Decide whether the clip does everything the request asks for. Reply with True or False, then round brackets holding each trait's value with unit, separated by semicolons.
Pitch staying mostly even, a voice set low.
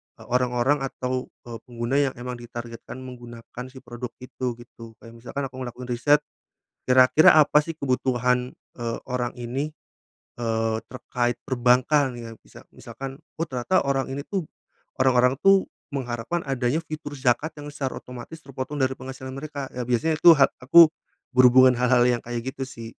True (2.3 semitones; 130 Hz)